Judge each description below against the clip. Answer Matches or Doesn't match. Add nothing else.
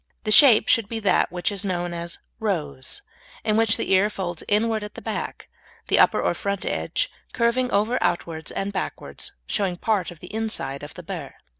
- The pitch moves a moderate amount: Matches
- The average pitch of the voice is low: Doesn't match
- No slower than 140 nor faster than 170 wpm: Doesn't match